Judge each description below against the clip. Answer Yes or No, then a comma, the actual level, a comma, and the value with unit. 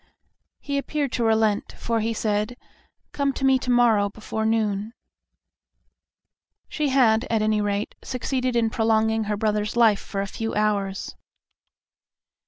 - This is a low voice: No, high, 220 Hz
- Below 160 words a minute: Yes, average, 140 wpm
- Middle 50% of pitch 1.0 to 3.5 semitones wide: Yes, narrow, 2.4 semitones